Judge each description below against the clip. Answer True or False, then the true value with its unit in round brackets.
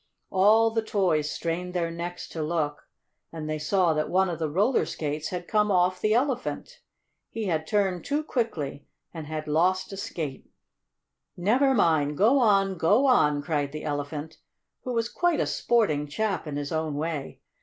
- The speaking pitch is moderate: True (175 Hz)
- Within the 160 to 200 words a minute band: True (175 wpm)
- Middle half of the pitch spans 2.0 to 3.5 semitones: False (5.5 semitones)